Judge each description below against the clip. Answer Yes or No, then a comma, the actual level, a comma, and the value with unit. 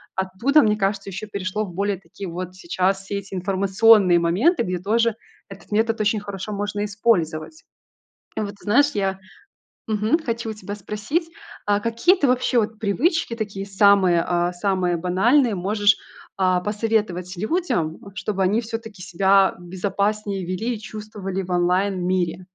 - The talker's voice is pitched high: Yes, high, 200 Hz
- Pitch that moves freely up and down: No, average, 2.8 semitones